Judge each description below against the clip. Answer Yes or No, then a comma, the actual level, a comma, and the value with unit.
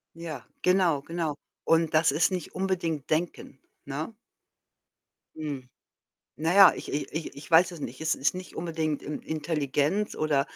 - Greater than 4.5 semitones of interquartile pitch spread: No, average, 2.7 semitones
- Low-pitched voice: No, medium, 160 Hz